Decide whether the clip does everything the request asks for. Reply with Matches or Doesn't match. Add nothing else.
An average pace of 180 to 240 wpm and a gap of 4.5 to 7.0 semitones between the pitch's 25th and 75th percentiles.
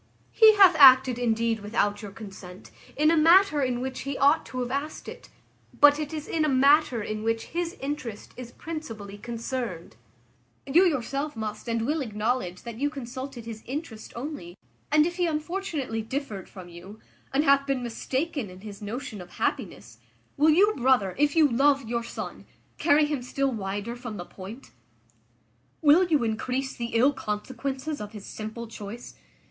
Doesn't match